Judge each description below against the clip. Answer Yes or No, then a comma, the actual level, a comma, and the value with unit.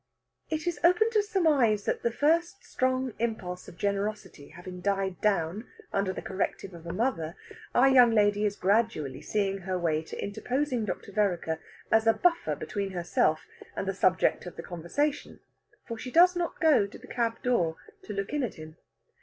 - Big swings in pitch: Yes, wide, 6.0 semitones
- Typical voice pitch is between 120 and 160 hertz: No, high, 210 Hz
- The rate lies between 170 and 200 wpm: Yes, average, 180 wpm